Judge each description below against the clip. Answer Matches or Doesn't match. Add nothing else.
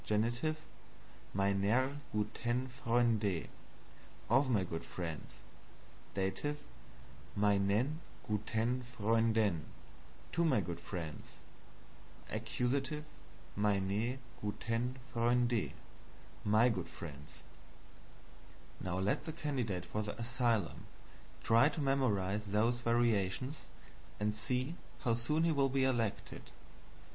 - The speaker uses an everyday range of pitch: Matches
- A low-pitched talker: Matches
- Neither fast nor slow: Doesn't match